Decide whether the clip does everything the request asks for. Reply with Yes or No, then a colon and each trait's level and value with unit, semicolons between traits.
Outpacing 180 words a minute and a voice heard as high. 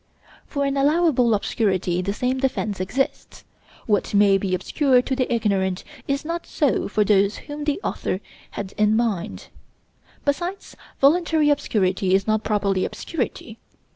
No: average, 140 wpm; high, 225 Hz